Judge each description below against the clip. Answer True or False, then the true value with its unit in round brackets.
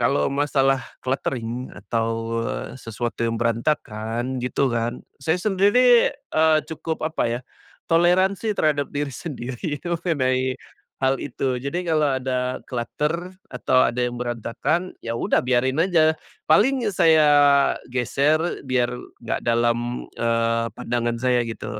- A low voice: True (130 Hz)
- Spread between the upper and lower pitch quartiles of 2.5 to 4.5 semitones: False (4.9 semitones)